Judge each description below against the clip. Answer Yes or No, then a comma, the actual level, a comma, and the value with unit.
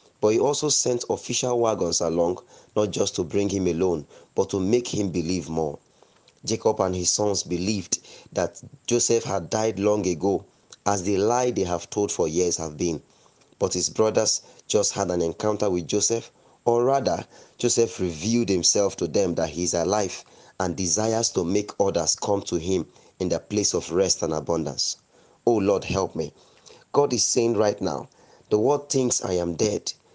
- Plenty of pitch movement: No, average, 4.6 semitones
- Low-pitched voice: Yes, low, 100 Hz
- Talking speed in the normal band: Yes, average, 180 wpm